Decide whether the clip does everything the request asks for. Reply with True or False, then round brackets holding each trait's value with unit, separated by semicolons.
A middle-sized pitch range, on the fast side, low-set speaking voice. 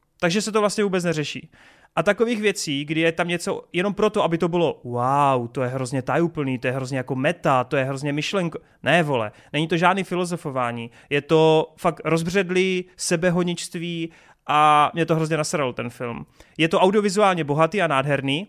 False (4.2 semitones; 180 wpm; 165 Hz)